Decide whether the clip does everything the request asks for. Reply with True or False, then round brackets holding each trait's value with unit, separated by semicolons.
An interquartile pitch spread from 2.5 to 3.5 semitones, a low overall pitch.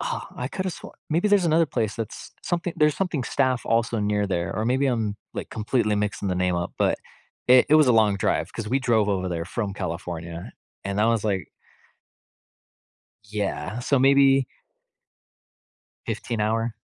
False (4.9 semitones; 110 Hz)